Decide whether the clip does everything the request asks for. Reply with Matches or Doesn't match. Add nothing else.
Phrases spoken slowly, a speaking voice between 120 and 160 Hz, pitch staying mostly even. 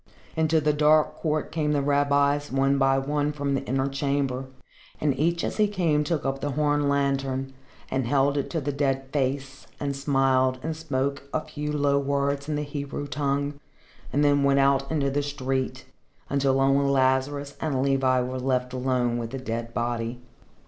Doesn't match